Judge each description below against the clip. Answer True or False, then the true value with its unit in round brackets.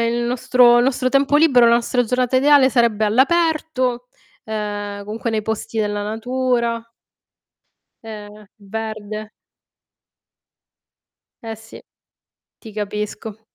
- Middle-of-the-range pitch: False (230 Hz)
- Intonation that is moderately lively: True (3.0 semitones)